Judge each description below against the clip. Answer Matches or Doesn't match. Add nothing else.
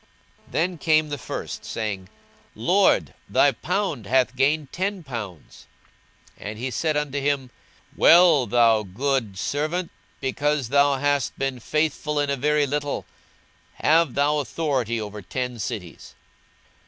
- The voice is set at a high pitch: Doesn't match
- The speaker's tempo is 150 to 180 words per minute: Doesn't match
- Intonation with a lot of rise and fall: Doesn't match